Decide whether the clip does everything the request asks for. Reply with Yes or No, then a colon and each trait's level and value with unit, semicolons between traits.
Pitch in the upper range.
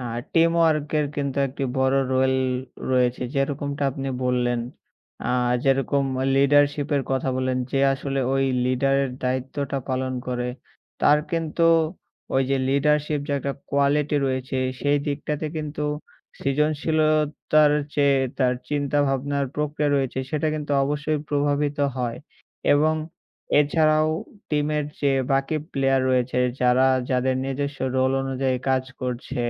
No: medium, 140 Hz